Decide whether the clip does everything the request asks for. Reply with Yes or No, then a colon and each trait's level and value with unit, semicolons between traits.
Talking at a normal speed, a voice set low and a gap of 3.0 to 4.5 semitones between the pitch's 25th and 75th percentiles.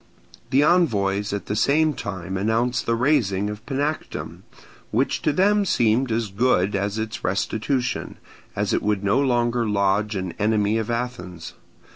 Yes: average, 150 wpm; low, 110 Hz; average, 4.1 semitones